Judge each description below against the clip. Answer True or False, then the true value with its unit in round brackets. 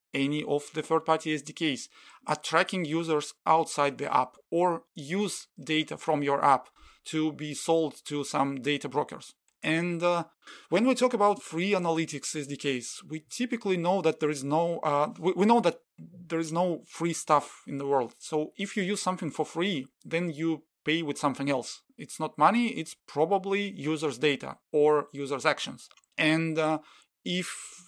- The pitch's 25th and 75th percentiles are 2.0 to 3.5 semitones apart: True (2.8 semitones)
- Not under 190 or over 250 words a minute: False (165 wpm)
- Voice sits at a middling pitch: True (160 Hz)